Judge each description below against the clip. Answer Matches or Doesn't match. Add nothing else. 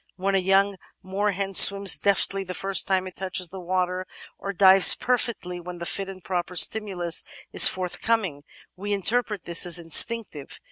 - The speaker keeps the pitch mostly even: Matches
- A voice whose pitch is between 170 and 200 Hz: Matches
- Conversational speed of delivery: Matches